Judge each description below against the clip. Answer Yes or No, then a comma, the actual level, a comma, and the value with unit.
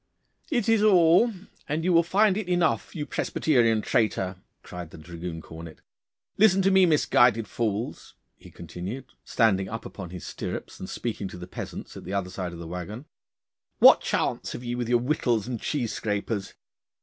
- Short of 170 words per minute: No, average, 175 wpm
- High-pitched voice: No, low, 115 Hz